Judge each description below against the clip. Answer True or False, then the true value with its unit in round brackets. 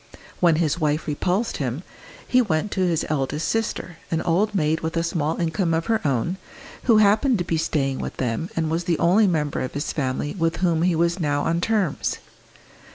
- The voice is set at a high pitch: False (165 Hz)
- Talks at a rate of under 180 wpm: False (200 wpm)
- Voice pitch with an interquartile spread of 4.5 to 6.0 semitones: False (3.3 semitones)